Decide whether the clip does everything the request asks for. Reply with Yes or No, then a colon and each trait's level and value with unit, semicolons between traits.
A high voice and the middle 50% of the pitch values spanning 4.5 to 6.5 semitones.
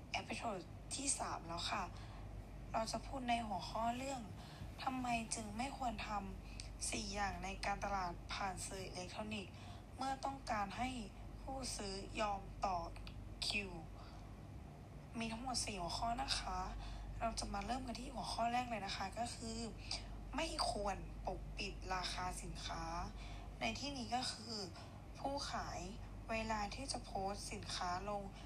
Yes: high, 225 Hz; average, 5.2 semitones